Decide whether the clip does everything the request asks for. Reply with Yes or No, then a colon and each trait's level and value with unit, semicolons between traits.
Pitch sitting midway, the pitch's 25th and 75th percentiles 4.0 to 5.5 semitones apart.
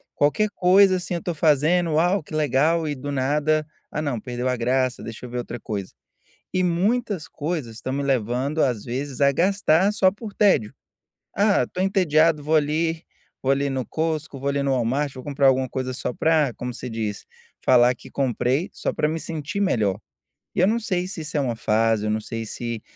Yes: medium, 145 Hz; average, 4.9 semitones